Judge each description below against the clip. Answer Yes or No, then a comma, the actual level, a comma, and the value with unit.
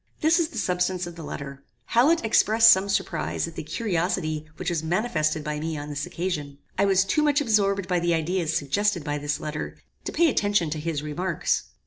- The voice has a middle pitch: Yes, medium, 175 Hz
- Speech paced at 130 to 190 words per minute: No, average, 200 wpm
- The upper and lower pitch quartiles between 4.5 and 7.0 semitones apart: Yes, average, 4.9 semitones